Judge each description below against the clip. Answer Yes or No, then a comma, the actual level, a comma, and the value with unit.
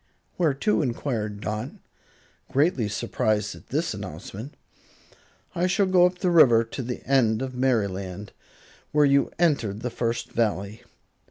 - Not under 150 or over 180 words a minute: No, average, 140 wpm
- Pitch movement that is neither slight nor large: No, wide, 5.7 semitones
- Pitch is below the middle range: Yes, low, 120 Hz